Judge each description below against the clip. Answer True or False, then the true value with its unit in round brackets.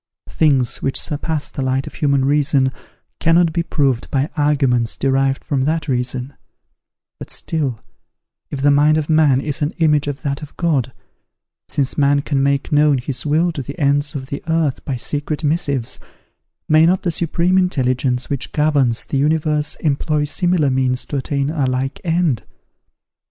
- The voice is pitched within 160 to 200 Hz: False (145 Hz)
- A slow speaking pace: False (165 wpm)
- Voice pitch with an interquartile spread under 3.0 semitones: True (2.6 semitones)